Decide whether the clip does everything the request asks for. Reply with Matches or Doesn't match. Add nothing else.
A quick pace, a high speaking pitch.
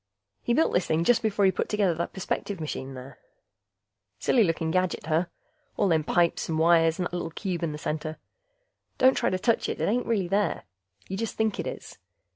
Doesn't match